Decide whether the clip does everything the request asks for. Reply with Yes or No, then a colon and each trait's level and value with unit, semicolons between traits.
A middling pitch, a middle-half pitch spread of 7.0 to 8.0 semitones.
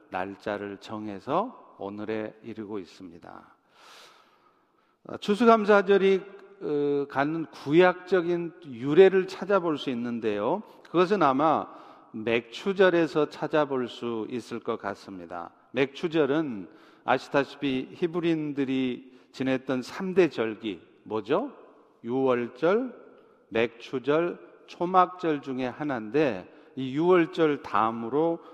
Yes: medium, 145 Hz; wide, 7.3 semitones